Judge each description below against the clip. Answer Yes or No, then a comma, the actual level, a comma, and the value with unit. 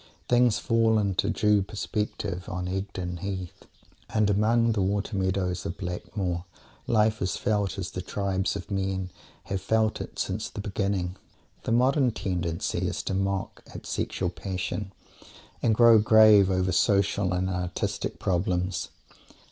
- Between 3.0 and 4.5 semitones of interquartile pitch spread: No, narrow, 2.5 semitones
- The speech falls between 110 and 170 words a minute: Yes, average, 140 wpm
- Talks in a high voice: No, low, 100 Hz